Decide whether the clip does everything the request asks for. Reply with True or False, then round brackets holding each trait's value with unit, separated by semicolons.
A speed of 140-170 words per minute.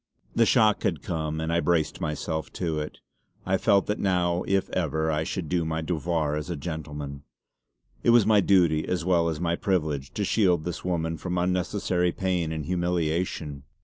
False (180 wpm)